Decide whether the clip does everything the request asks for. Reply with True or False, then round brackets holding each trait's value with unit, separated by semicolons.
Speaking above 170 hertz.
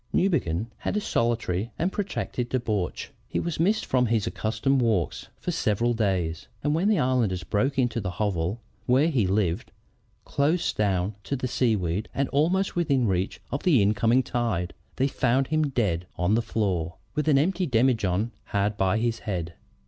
False (115 Hz)